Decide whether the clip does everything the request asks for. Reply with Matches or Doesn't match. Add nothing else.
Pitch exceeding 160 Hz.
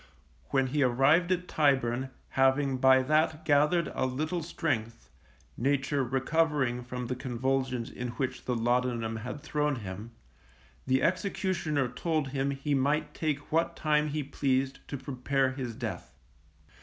Doesn't match